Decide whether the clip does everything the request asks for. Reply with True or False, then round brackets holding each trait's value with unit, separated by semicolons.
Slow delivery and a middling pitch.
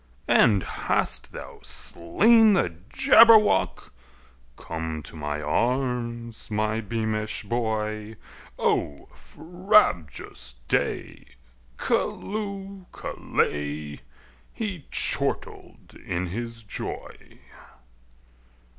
False (75 wpm; 110 Hz)